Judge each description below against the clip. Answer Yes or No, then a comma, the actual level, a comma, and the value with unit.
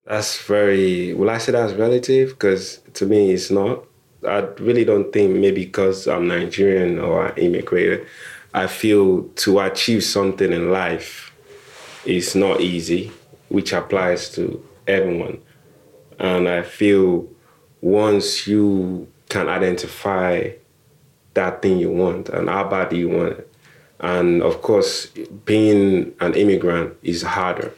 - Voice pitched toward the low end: Yes, very low, 95 Hz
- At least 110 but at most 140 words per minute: Yes, slow, 135 wpm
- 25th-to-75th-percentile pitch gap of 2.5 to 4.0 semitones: Yes, average, 2.8 semitones